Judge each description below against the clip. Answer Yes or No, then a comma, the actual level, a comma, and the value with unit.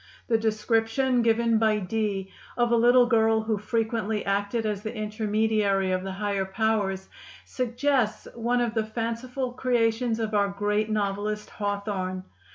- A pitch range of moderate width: No, narrow, 2.2 semitones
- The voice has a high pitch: Yes, high, 220 Hz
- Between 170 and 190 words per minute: No, average, 145 wpm